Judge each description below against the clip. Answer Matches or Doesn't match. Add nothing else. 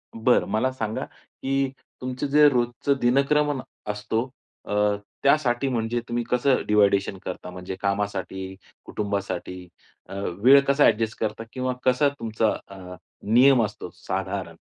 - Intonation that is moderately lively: Matches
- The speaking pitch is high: Doesn't match